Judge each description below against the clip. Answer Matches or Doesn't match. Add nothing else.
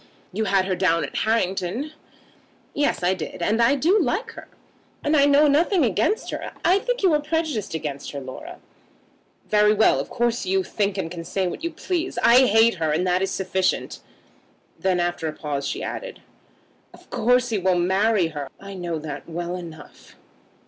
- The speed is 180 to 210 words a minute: Matches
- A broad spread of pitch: Matches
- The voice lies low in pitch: Doesn't match